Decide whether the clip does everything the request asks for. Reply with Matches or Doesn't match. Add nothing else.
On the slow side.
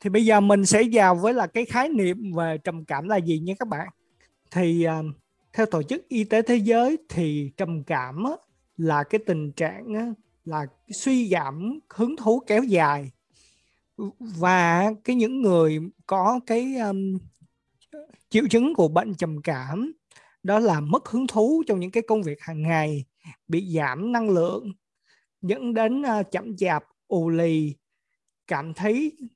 Matches